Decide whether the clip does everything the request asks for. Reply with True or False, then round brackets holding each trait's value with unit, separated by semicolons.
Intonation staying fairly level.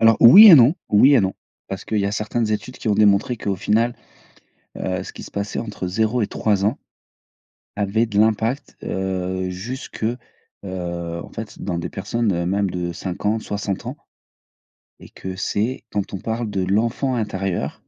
False (3.0 semitones)